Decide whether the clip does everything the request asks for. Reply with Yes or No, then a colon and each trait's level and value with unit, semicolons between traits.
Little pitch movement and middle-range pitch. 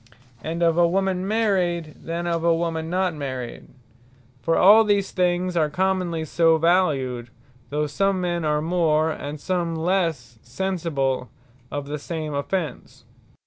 No: average, 3.3 semitones; medium, 165 Hz